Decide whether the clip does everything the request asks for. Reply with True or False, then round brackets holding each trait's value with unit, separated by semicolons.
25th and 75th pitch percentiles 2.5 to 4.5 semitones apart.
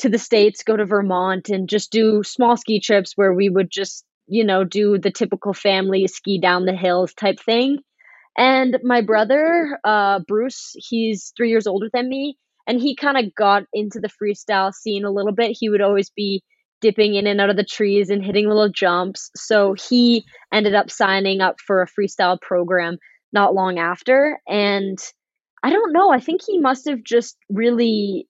True (3.3 semitones)